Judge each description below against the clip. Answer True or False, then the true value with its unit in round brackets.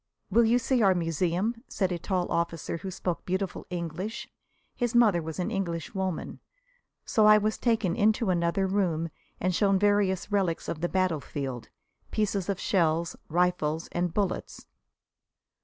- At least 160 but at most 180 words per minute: False (145 wpm)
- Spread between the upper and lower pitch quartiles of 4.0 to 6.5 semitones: False (3.3 semitones)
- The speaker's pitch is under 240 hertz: True (185 Hz)